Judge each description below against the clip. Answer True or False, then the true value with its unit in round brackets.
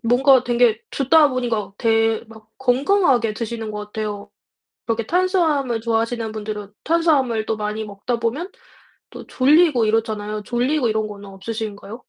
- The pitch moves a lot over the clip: False (3.4 semitones)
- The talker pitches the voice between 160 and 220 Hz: False (230 Hz)